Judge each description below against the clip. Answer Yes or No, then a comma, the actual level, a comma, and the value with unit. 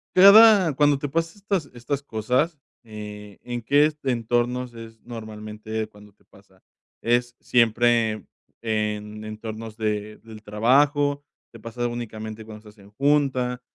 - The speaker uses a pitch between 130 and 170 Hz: No, low, 115 Hz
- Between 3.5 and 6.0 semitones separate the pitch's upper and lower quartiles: Yes, average, 4.2 semitones